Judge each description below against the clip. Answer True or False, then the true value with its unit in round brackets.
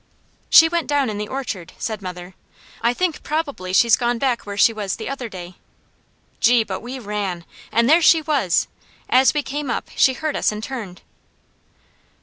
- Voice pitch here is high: True (235 Hz)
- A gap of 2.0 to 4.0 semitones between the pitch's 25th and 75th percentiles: False (5.4 semitones)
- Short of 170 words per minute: False (180 wpm)